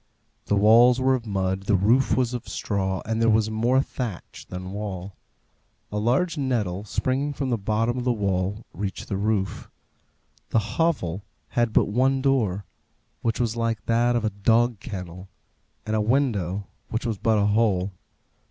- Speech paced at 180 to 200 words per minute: No, average, 170 wpm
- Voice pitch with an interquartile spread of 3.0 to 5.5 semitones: Yes, average, 3.5 semitones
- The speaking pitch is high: No, low, 110 Hz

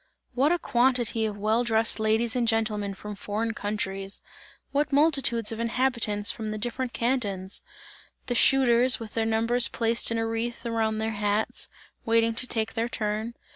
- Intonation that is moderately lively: No, narrow, 1.9 semitones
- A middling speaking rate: Yes, average, 165 wpm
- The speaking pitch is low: No, high, 225 Hz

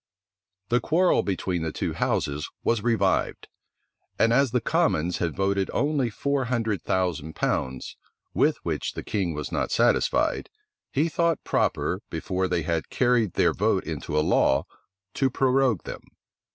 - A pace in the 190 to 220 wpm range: No, average, 150 wpm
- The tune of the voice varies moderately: No, wide, 7.3 semitones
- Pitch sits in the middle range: No, low, 105 Hz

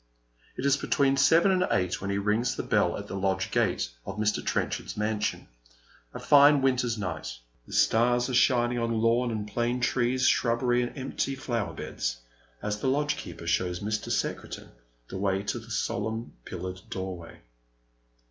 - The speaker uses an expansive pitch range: No, average, 4.4 semitones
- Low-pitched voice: Yes, low, 115 Hz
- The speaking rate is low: No, average, 165 wpm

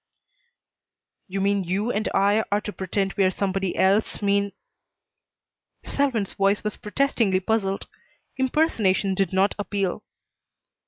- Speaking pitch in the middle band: No, high, 200 Hz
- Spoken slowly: Yes, slow, 125 wpm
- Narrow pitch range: Yes, narrow, 1.6 semitones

